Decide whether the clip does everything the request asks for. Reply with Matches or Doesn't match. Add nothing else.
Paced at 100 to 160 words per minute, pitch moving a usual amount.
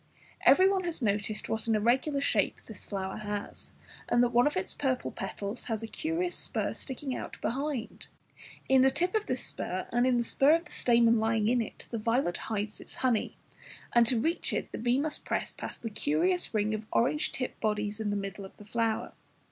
Doesn't match